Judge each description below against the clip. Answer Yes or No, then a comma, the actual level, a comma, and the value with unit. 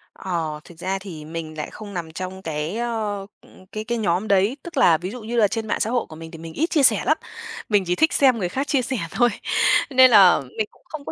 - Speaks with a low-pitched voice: No, high, 200 Hz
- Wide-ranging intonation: Yes, wide, 5.9 semitones